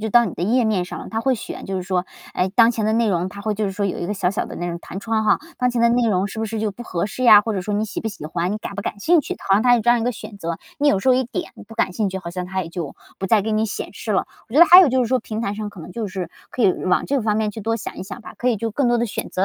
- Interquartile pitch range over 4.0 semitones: No, average, 3.5 semitones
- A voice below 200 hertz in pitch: No, high, 215 Hz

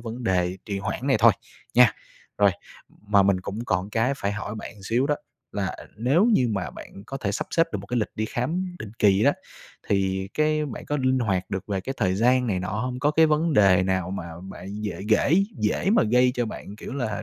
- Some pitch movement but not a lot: Yes, average, 4.7 semitones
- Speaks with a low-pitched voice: Yes, low, 110 Hz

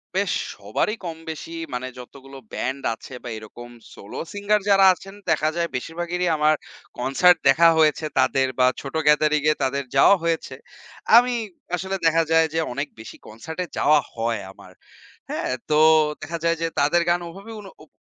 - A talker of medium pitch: Yes, medium, 155 Hz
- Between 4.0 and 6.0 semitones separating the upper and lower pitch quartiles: Yes, average, 4.3 semitones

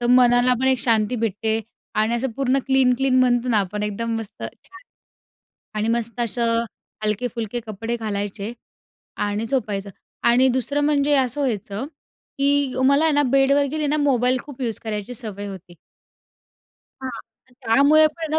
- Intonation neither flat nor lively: Yes, average, 3.7 semitones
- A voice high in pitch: Yes, high, 245 Hz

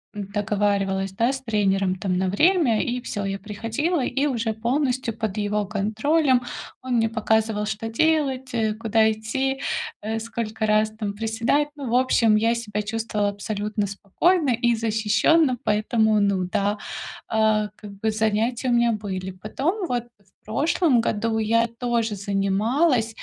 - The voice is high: Yes, high, 220 Hz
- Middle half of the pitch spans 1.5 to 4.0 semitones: Yes, average, 2.8 semitones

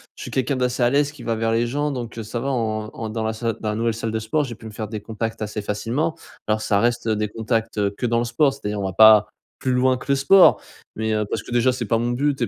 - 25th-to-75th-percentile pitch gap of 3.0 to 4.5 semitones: No, narrow, 2.6 semitones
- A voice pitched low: Yes, low, 115 Hz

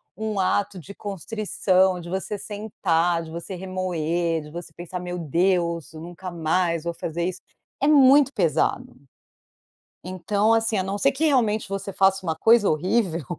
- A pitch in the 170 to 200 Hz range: Yes, medium, 185 Hz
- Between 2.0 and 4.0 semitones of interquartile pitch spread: Yes, average, 3.3 semitones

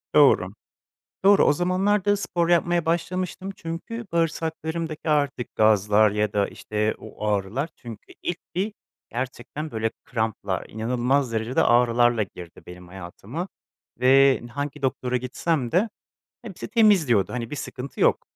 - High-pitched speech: No, low, 135 Hz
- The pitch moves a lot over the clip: Yes, wide, 7.3 semitones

